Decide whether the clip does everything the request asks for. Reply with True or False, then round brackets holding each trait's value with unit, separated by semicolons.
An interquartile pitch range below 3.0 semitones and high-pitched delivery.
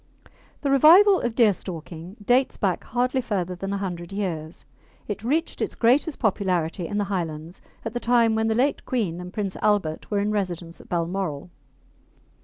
False (5.2 semitones; 200 Hz)